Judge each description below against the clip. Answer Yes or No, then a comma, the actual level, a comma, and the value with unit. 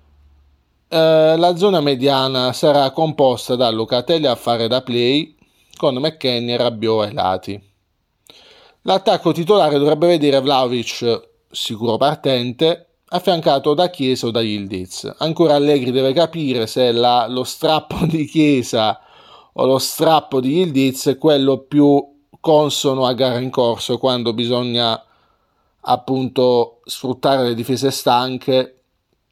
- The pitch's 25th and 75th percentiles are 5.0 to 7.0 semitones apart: No, average, 3.8 semitones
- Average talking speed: Yes, average, 125 wpm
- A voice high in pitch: No, low, 130 Hz